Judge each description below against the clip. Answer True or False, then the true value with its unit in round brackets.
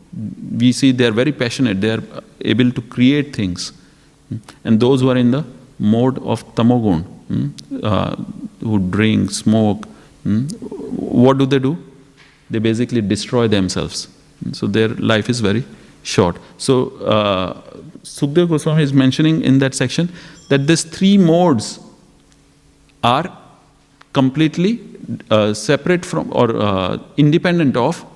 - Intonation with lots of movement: False (5.0 semitones)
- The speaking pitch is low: True (130 Hz)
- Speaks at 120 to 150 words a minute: True (135 wpm)